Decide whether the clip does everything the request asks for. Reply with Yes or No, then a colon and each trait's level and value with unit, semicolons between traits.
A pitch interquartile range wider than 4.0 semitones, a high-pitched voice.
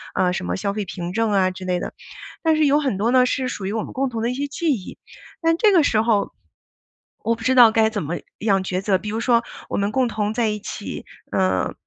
Yes: average, 4.7 semitones; high, 220 Hz